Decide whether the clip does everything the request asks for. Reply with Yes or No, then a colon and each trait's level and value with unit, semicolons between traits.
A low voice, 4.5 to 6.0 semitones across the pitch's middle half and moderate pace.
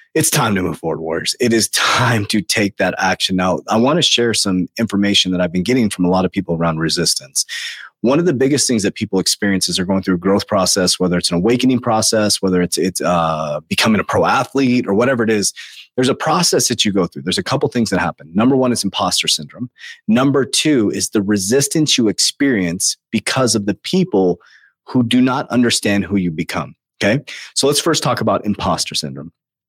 No: low, 105 Hz; average, 4.9 semitones; fast, 215 wpm